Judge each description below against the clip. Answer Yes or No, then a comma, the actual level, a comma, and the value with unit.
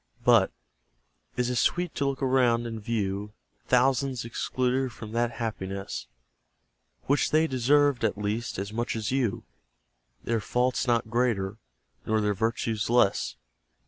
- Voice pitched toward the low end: Yes, low, 115 Hz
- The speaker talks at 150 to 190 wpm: No, slow, 135 wpm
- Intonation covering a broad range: No, average, 2.8 semitones